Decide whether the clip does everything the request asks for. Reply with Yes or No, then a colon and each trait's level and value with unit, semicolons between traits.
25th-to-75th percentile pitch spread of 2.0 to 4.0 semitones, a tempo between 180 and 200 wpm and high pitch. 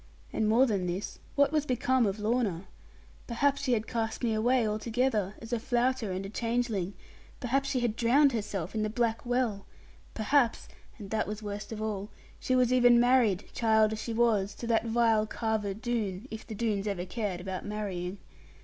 Yes: average, 2.8 semitones; average, 185 wpm; high, 220 Hz